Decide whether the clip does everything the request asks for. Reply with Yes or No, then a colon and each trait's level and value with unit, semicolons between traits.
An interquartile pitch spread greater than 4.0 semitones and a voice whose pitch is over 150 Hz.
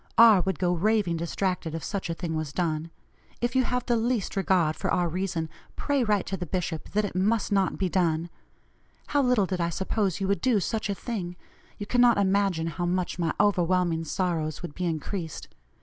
No: average, 3.5 semitones; medium, 185 Hz